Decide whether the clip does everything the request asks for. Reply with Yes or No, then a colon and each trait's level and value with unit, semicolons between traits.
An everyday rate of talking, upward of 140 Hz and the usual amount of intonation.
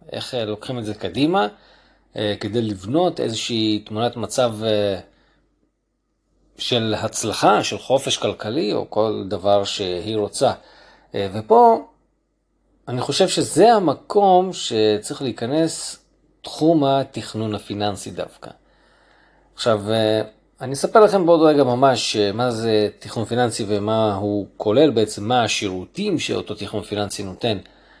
No: average, 110 wpm; low, 110 Hz; average, 3.9 semitones